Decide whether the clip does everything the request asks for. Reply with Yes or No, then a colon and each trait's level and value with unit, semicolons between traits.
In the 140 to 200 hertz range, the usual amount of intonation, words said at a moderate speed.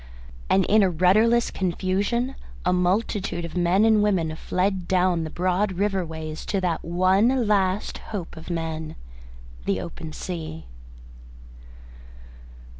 No: medium, 185 Hz; average, 3.3 semitones; slow, 125 wpm